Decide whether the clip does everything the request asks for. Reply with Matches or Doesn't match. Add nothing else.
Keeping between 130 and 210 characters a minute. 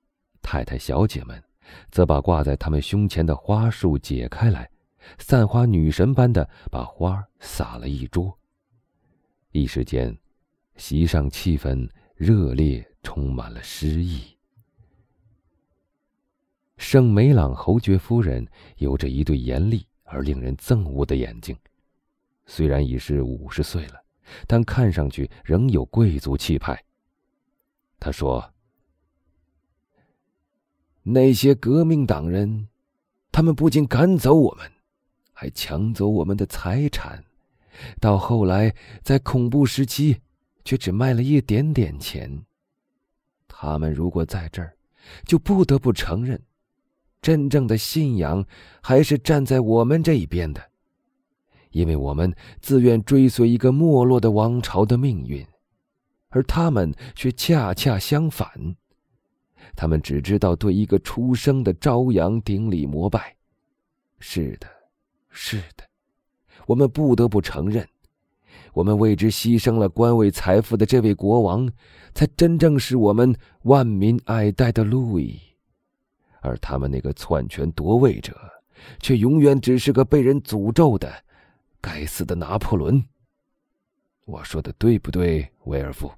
Matches